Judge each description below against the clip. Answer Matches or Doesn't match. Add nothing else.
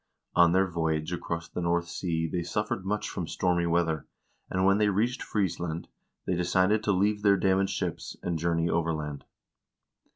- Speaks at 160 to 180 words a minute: Matches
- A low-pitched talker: Matches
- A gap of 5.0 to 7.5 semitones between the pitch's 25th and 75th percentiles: Doesn't match